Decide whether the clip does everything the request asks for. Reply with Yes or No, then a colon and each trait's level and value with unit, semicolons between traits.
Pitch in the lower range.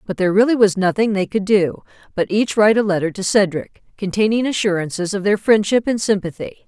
No: high, 200 Hz